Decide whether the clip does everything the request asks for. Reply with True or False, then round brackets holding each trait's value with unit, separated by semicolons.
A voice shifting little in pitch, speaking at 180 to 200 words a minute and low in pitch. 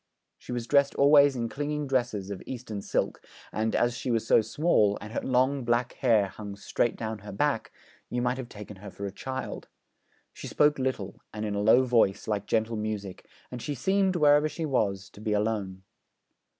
False (4.3 semitones; 195 wpm; 115 Hz)